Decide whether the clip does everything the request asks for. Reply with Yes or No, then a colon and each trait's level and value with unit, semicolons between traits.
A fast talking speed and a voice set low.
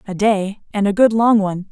No: fast, 245 wpm; high, 205 Hz